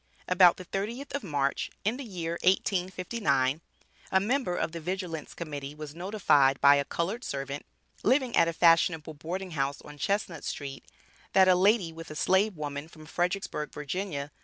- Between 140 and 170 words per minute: Yes, average, 165 wpm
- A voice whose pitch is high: No, medium, 170 Hz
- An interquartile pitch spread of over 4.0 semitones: Yes, average, 4.5 semitones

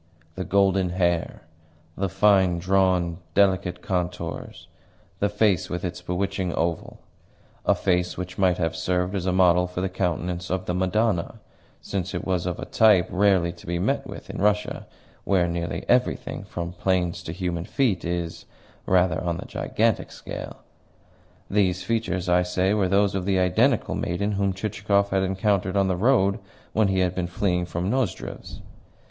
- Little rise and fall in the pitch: Yes, narrow, 1.8 semitones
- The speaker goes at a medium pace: Yes, average, 165 wpm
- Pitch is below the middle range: Yes, very low, 90 Hz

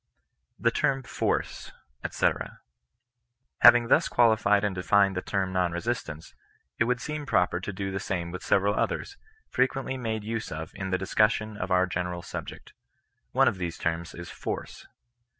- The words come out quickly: No, average, 165 wpm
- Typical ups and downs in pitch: Yes, average, 4.0 semitones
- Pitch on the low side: Yes, low, 100 Hz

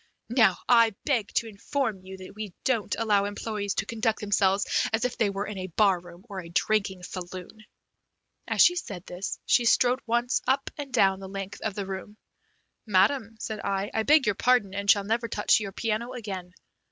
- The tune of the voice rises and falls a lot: No, average, 3.0 semitones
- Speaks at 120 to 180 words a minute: No, average, 195 wpm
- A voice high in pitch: Yes, high, 205 Hz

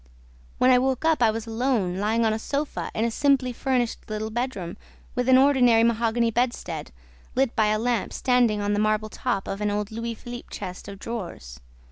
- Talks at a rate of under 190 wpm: No, average, 195 wpm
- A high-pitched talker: Yes, high, 230 Hz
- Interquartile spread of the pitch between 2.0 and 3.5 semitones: Yes, average, 2.7 semitones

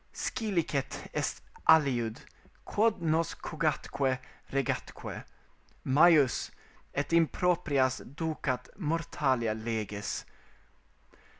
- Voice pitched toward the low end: No, medium, 145 Hz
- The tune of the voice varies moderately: Yes, average, 4.3 semitones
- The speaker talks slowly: Yes, slow, 75 wpm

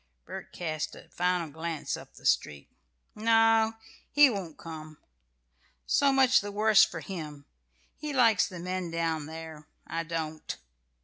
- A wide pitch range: Yes, wide, 5.7 semitones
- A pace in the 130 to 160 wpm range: Yes, average, 145 wpm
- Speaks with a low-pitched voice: No, medium, 170 Hz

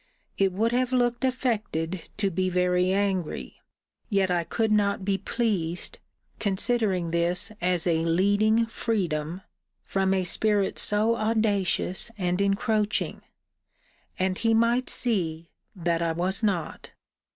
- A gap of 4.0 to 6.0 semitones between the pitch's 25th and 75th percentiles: No, average, 3.5 semitones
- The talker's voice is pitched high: Yes, high, 195 Hz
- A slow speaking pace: Yes, slow, 125 wpm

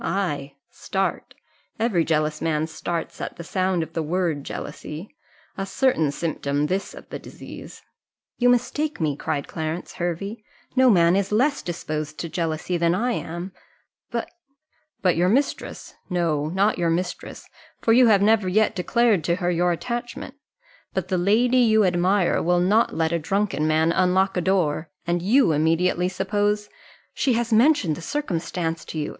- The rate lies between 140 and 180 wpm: Yes, average, 165 wpm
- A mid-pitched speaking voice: Yes, medium, 180 Hz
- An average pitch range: Yes, average, 4.3 semitones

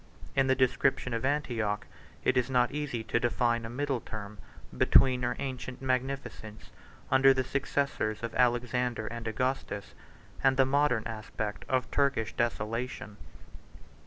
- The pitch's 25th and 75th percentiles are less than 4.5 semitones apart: Yes, average, 2.8 semitones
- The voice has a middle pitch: No, low, 125 Hz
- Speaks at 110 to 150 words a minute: Yes, average, 140 wpm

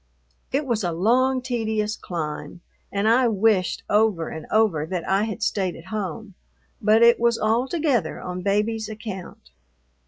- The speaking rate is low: No, average, 150 wpm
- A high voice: Yes, high, 215 Hz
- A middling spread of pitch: Yes, average, 3.6 semitones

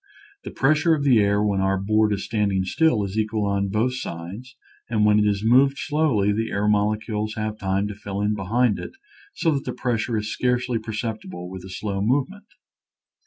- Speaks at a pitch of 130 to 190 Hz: No, low, 105 Hz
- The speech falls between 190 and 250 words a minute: Yes, average, 200 wpm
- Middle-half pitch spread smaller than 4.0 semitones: Yes, average, 3.4 semitones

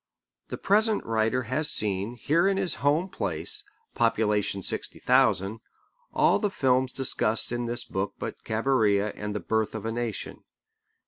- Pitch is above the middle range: No, low, 115 Hz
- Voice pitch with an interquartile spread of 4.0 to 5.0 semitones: Yes, average, 4.4 semitones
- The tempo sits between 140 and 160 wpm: Yes, average, 150 wpm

